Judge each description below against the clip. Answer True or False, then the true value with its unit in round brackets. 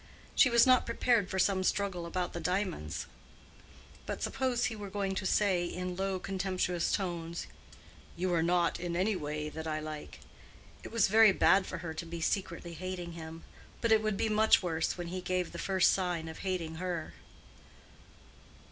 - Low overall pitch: False (180 Hz)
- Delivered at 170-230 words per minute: True (180 wpm)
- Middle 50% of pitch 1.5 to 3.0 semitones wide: True (2.6 semitones)